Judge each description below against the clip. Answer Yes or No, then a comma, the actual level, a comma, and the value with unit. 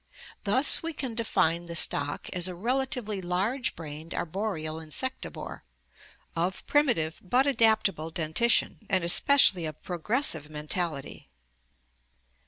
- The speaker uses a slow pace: Yes, slow, 120 wpm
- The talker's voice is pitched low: No, medium, 185 Hz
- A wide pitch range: Yes, wide, 6.7 semitones